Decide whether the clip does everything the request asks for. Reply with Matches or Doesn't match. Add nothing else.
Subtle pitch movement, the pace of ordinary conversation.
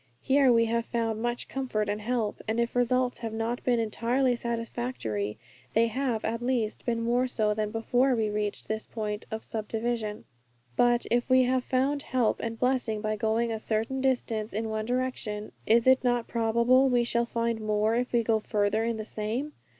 Matches